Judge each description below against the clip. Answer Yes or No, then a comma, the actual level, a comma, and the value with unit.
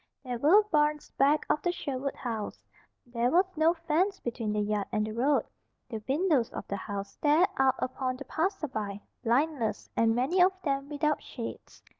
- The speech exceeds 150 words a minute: Yes, average, 175 wpm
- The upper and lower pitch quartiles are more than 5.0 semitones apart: Yes, wide, 5.4 semitones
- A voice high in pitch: Yes, very high, 275 Hz